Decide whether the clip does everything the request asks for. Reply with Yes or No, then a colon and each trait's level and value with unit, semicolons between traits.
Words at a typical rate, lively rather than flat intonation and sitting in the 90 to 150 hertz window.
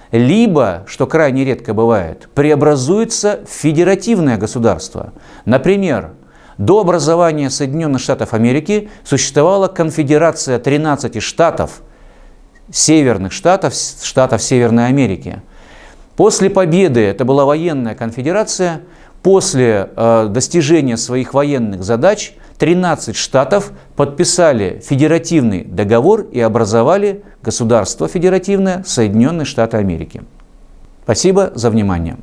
No: slow, 95 wpm; wide, 6.9 semitones; medium, 140 Hz